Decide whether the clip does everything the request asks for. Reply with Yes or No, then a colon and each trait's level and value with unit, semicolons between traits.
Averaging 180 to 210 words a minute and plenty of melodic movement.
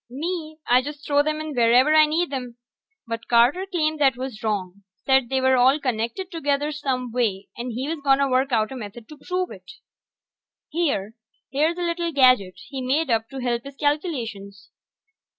No: average, 185 wpm; average, 4.4 semitones